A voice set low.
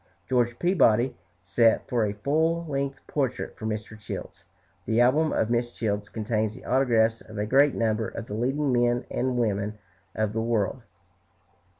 Yes: low, 120 Hz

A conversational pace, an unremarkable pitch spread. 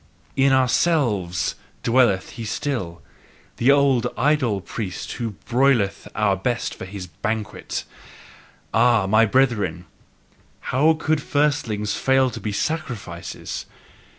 No: slow, 110 wpm; average, 5.0 semitones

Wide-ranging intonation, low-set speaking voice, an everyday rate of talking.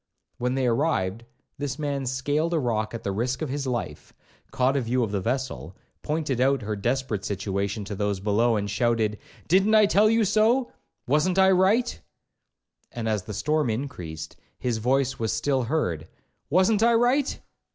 Yes: wide, 6.4 semitones; low, 130 Hz; average, 170 wpm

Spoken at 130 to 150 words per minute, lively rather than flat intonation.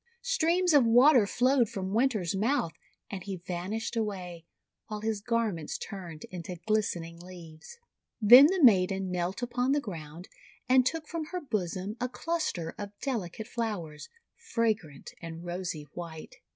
Yes: average, 145 wpm; wide, 5.9 semitones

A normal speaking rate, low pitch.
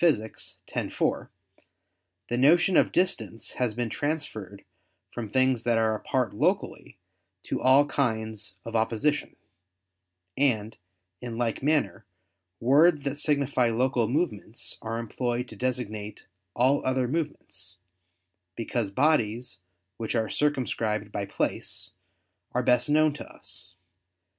No: slow, 120 wpm; low, 120 Hz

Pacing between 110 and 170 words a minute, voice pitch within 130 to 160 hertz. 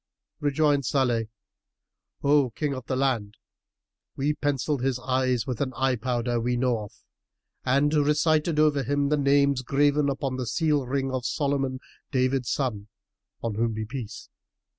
Yes: average, 155 wpm; low, 135 Hz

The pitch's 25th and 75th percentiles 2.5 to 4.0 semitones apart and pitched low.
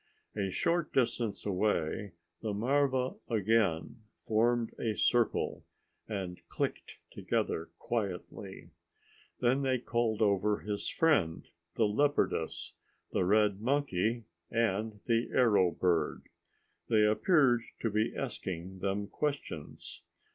Yes: average, 3.4 semitones; low, 110 Hz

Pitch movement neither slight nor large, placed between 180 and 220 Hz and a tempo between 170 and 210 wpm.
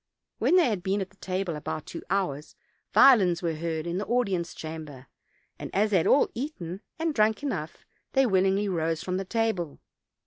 Yes: average, 4.6 semitones; high, 190 Hz; average, 175 wpm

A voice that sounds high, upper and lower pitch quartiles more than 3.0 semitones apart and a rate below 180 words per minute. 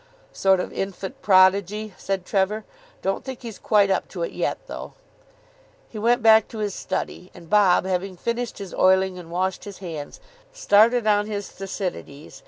No: high, 195 Hz; narrow, 2.5 semitones; average, 170 wpm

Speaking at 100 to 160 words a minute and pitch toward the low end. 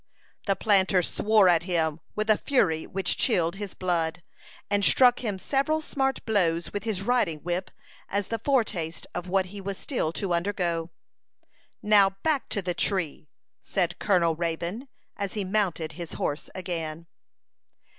No: average, 155 wpm; high, 190 Hz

